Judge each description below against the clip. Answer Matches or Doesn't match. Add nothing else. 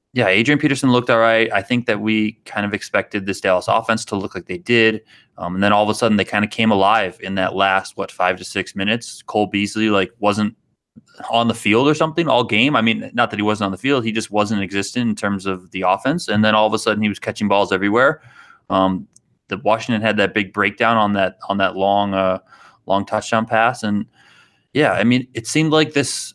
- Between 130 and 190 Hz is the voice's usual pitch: Doesn't match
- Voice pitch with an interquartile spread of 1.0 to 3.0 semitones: Matches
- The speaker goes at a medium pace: Doesn't match